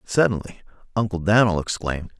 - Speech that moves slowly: Yes, slow, 110 wpm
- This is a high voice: No, very low, 95 Hz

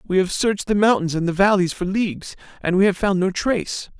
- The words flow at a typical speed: No, fast, 240 wpm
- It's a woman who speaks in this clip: No, male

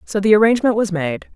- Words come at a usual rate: No, fast, 220 wpm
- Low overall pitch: No, high, 205 Hz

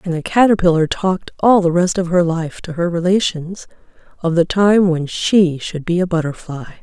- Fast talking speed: No, average, 195 wpm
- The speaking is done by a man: No, female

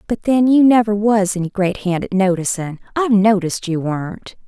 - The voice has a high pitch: Yes, high, 200 Hz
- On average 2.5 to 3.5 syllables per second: No, 5.4 syllables/s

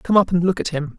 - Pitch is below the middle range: No, medium, 180 Hz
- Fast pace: Yes, fast, 365 wpm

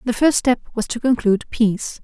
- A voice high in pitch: Yes, high, 235 Hz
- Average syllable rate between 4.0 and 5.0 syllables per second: No, 6.0 syllables/s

